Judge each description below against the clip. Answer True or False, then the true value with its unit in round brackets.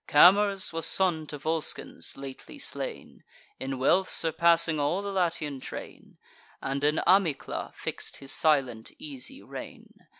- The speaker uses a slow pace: True (130 wpm)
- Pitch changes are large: False (4.7 semitones)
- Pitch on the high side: False (160 Hz)